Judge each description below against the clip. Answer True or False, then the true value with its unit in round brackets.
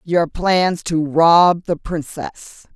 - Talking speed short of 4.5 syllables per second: True (2.7 syllables/s)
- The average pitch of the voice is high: False (165 Hz)